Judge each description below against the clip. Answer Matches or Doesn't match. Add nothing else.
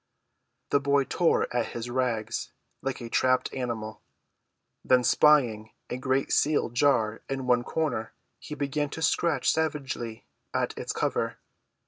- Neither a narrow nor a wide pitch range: Matches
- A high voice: Doesn't match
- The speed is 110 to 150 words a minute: Matches